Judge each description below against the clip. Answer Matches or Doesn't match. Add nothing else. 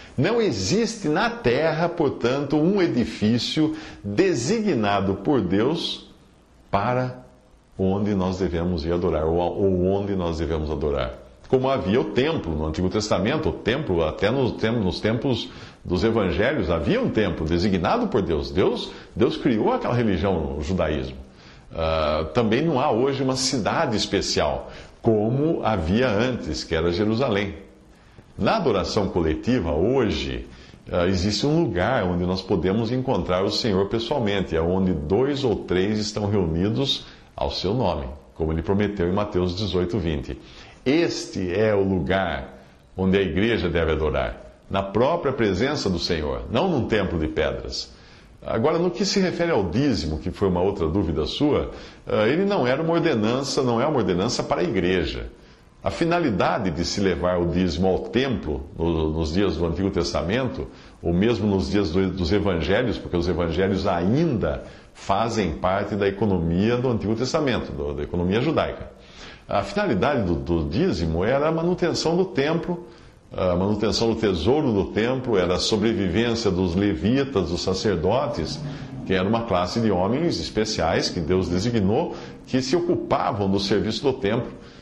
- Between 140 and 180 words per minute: Matches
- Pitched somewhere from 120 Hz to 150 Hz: Doesn't match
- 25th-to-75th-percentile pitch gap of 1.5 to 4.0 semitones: Doesn't match